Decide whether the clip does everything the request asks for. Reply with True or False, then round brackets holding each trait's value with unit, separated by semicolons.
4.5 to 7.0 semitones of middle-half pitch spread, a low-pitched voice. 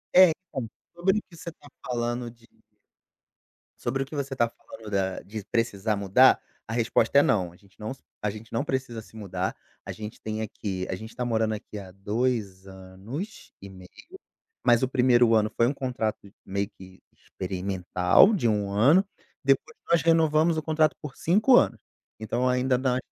True (5.1 semitones; 115 Hz)